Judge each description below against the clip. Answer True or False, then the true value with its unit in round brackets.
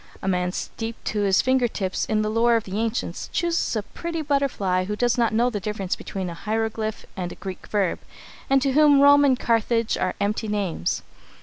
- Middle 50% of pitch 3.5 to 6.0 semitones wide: True (4.1 semitones)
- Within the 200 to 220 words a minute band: True (205 wpm)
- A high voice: True (220 Hz)